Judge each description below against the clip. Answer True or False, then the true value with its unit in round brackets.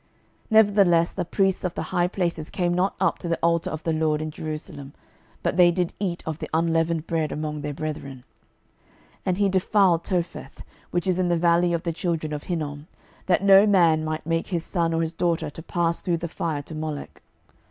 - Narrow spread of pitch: True (2.3 semitones)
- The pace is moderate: False (210 wpm)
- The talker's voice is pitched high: False (170 Hz)